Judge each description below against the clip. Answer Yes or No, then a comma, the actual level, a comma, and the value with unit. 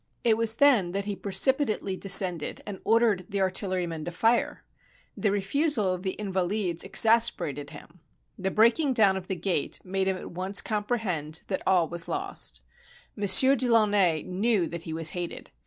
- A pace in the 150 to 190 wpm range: Yes, average, 165 wpm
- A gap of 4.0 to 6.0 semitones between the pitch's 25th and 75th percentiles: No, average, 3.6 semitones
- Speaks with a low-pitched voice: No, high, 190 Hz